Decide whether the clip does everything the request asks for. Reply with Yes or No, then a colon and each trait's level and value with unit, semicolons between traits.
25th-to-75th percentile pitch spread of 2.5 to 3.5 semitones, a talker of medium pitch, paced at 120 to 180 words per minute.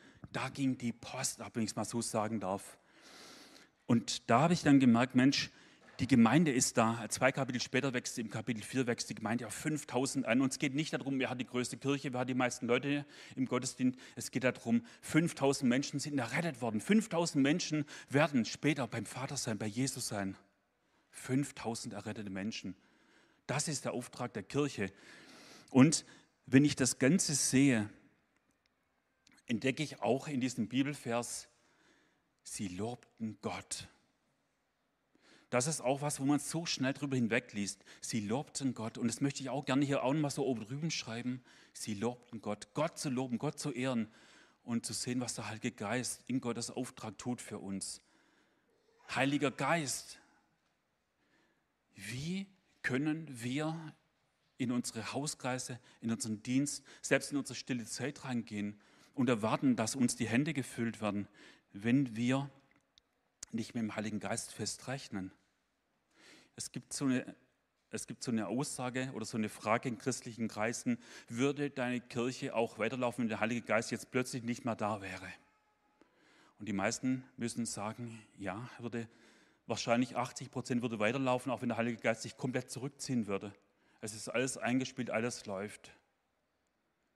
No: average, 3.2 semitones; low, 125 Hz; average, 160 wpm